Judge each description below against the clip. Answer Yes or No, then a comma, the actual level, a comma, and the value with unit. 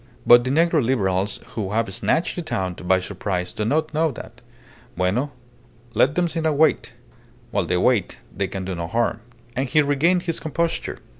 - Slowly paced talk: No, average, 180 wpm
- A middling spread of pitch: No, wide, 8.7 semitones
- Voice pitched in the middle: No, low, 120 Hz